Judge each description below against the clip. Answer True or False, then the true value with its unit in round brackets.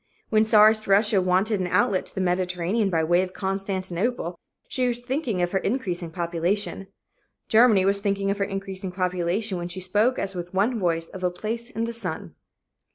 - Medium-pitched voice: False (195 Hz)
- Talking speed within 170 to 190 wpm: True (185 wpm)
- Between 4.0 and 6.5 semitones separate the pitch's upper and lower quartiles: False (3.2 semitones)